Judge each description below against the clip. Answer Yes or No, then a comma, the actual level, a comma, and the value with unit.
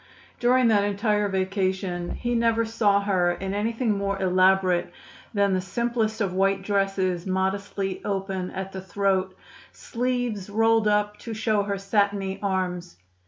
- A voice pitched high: Yes, high, 200 Hz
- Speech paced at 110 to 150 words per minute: Yes, average, 140 wpm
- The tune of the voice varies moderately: No, narrow, 2.1 semitones